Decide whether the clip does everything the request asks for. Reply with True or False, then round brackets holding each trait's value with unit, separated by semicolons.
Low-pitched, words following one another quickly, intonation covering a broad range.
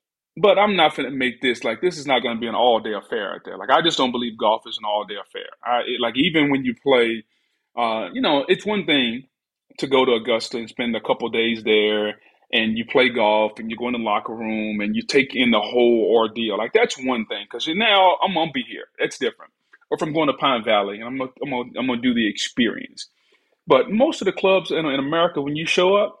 True (130 Hz; 265 wpm; 8.5 semitones)